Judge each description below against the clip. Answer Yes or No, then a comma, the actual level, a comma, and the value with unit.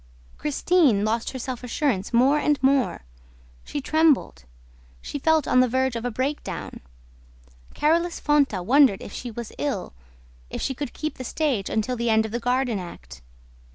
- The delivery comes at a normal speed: Yes, average, 165 wpm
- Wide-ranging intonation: No, average, 4.3 semitones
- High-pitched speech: Yes, very high, 255 Hz